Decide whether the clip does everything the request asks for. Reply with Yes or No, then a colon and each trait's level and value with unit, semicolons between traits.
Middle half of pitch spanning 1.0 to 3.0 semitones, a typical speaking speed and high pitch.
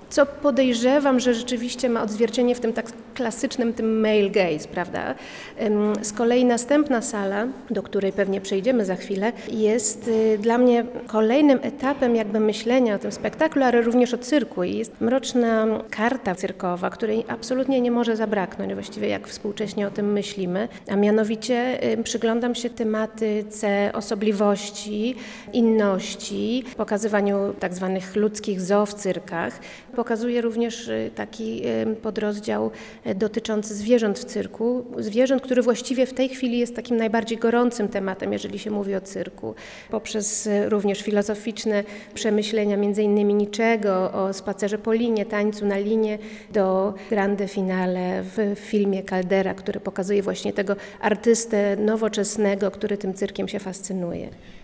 Yes: narrow, 2.5 semitones; average, 135 wpm; high, 215 Hz